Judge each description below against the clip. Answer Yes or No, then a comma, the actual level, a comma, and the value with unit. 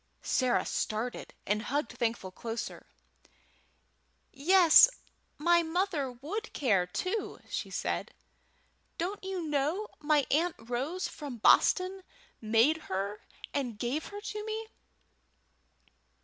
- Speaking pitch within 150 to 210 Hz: No, very high, 295 Hz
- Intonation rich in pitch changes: Yes, wide, 7.5 semitones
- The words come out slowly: Yes, slow, 105 wpm